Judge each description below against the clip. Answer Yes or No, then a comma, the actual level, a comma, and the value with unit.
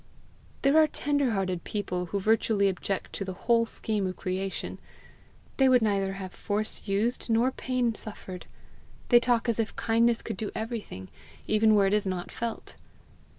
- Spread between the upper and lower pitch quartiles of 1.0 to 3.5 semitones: Yes, average, 3.2 semitones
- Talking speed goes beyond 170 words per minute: No, average, 165 wpm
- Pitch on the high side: Yes, high, 215 Hz